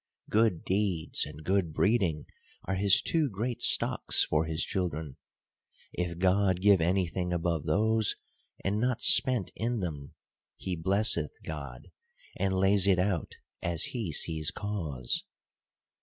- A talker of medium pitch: No, very low, 95 Hz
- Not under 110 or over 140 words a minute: Yes, slow, 135 wpm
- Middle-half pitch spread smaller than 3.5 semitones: No, average, 4.0 semitones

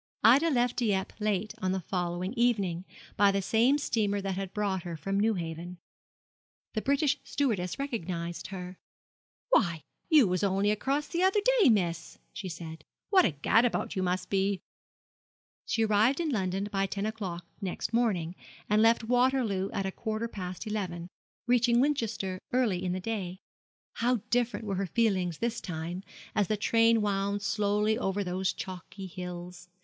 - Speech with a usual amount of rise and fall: Yes, average, 3.9 semitones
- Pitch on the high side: Yes, high, 200 Hz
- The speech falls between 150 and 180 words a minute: Yes, average, 160 wpm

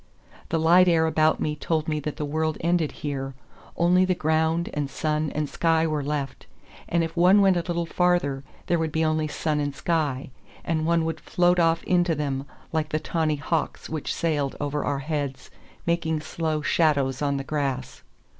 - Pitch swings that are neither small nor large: No, narrow, 2.3 semitones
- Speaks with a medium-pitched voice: Yes, medium, 155 Hz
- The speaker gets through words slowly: No, average, 185 wpm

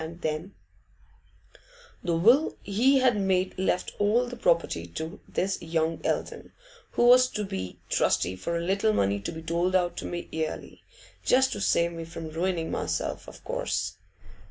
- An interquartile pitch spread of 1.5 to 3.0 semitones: No, average, 4.4 semitones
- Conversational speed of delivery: Yes, average, 165 wpm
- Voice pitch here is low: No, medium, 175 Hz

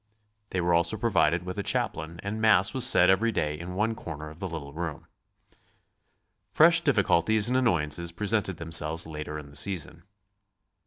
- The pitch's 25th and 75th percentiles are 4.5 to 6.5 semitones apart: Yes, average, 5.1 semitones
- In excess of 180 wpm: No, average, 165 wpm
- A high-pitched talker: No, very low, 85 Hz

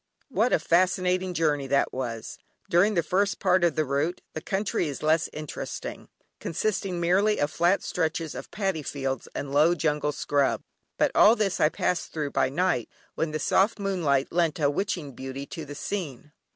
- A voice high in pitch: No, medium, 160 Hz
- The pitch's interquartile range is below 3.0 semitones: No, average, 4.4 semitones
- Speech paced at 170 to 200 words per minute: Yes, average, 180 wpm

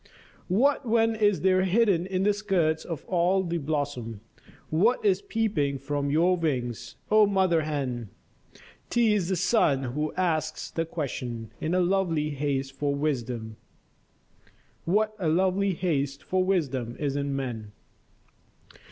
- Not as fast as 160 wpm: Yes, average, 140 wpm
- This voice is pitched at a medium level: Yes, medium, 165 Hz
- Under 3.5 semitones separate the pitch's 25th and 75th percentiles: No, wide, 5.4 semitones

